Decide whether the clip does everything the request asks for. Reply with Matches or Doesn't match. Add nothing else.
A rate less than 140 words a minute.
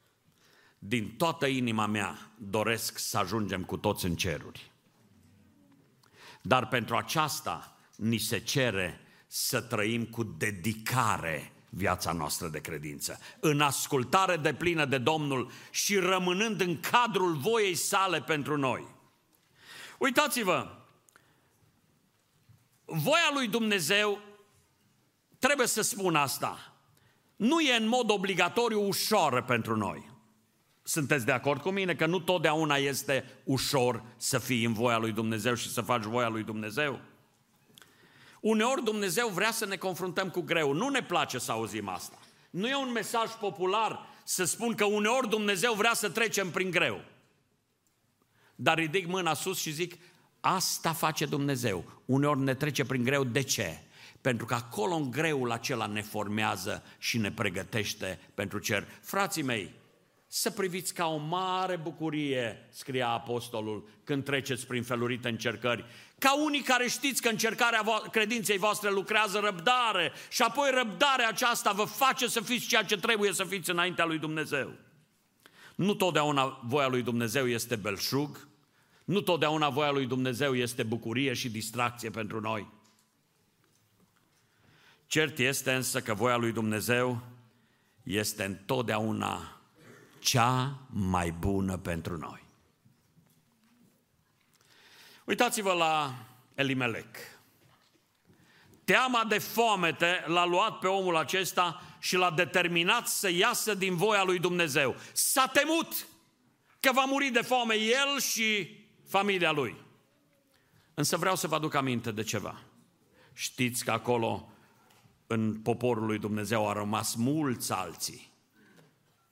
Matches